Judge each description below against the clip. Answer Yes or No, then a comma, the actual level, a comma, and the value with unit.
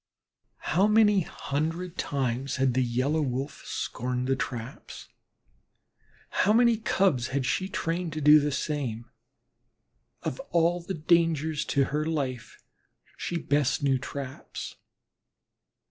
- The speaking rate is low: Yes, slow, 120 wpm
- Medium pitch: Yes, medium, 150 Hz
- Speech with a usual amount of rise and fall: Yes, average, 4.4 semitones